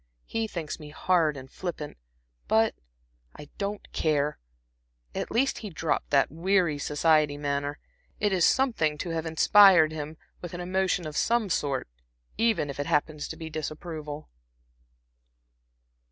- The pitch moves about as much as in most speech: Yes, average, 4.1 semitones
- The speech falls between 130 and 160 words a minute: Yes, average, 140 wpm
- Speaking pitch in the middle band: Yes, medium, 160 Hz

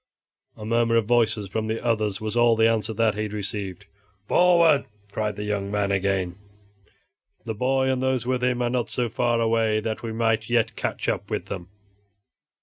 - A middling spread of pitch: No, narrow, 2.3 semitones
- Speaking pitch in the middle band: No, low, 110 Hz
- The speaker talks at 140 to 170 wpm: No, average, 190 wpm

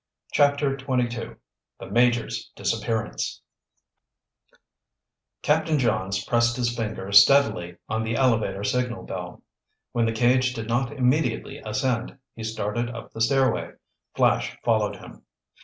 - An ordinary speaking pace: No, slow, 120 wpm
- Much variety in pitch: No, narrow, 2.5 semitones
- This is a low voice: Yes, low, 120 Hz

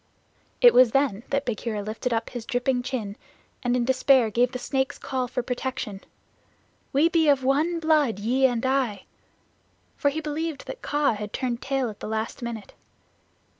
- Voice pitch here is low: No, very high, 255 Hz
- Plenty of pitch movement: No, average, 3.2 semitones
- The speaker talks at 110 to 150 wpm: No, average, 170 wpm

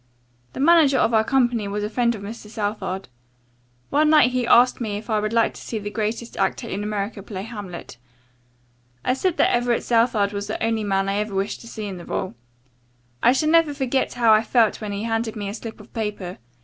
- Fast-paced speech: Yes, fast, 220 wpm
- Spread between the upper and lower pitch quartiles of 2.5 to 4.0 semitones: Yes, average, 2.8 semitones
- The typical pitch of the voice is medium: No, high, 220 Hz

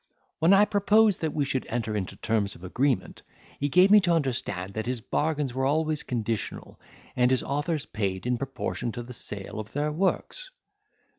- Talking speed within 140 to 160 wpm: No, average, 180 wpm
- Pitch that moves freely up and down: Yes, wide, 5.8 semitones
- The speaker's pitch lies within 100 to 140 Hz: Yes, low, 135 Hz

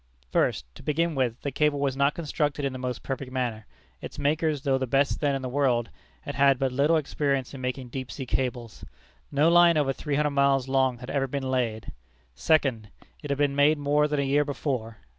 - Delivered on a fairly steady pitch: Yes, narrow, 2.2 semitones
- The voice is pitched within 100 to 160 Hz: Yes, medium, 140 Hz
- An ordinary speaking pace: No, fast, 215 wpm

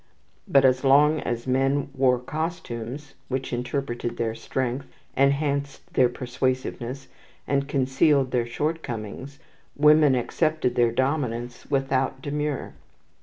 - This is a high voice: No, low, 135 Hz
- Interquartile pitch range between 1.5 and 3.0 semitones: Yes, narrow, 2.4 semitones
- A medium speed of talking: No, slow, 110 wpm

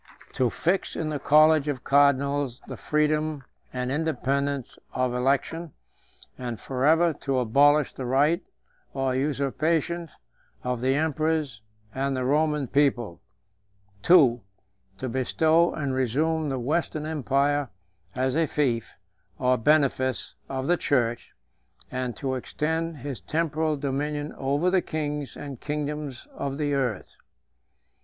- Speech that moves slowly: Yes, slow, 125 wpm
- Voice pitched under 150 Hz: Yes, medium, 140 Hz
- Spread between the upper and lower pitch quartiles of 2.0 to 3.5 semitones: Yes, average, 2.9 semitones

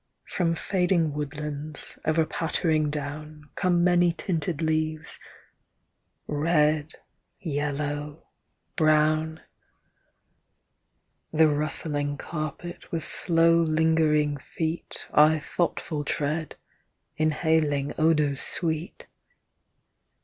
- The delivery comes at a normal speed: No, slow, 75 wpm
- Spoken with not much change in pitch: Yes, narrow, 1.6 semitones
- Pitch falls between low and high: Yes, medium, 155 Hz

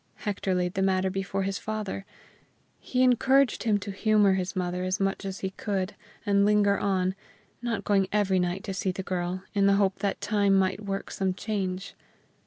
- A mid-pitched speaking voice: No, high, 195 Hz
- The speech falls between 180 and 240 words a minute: Yes, average, 190 wpm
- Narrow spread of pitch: Yes, narrow, 1.6 semitones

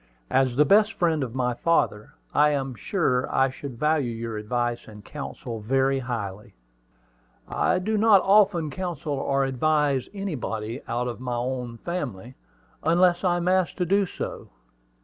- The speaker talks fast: No, average, 155 wpm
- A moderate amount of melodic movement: No, wide, 6.2 semitones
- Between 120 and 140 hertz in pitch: Yes, low, 135 Hz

